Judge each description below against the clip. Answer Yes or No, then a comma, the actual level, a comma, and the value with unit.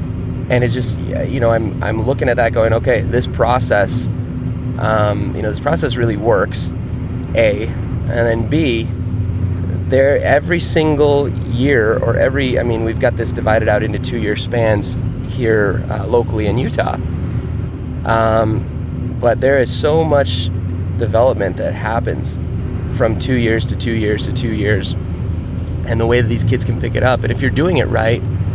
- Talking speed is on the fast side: No, average, 170 wpm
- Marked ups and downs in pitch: No, average, 2.9 semitones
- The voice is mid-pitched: No, low, 115 Hz